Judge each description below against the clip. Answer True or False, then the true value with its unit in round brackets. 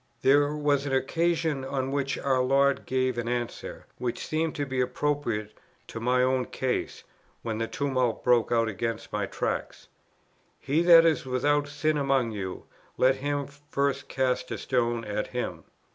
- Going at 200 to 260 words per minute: False (160 wpm)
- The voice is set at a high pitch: False (130 Hz)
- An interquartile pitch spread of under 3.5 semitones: True (2.9 semitones)